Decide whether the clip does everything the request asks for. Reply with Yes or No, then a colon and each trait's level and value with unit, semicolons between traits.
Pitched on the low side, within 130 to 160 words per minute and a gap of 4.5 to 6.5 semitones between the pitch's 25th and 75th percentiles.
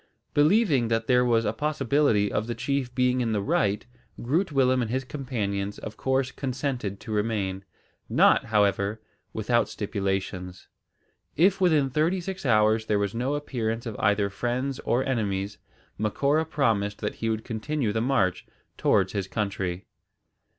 Yes: low, 115 Hz; average, 150 wpm; average, 4.8 semitones